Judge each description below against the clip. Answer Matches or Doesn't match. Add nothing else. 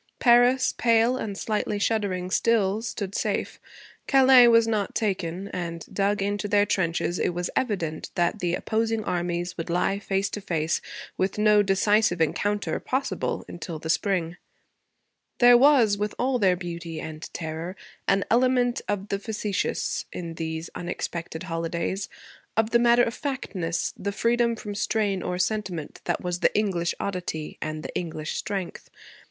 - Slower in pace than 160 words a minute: Matches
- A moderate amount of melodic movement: Matches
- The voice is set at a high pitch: Matches